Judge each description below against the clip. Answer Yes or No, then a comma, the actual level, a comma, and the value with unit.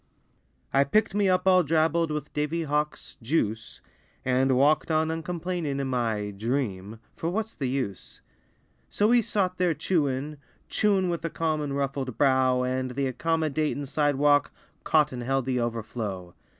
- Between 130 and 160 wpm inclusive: Yes, average, 150 wpm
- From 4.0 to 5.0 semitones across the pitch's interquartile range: Yes, average, 4.3 semitones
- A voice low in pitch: No, medium, 145 Hz